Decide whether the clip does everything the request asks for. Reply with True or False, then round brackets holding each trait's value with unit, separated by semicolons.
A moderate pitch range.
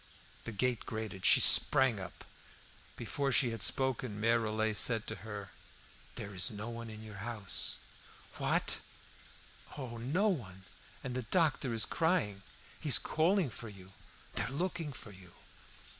True (4.1 semitones)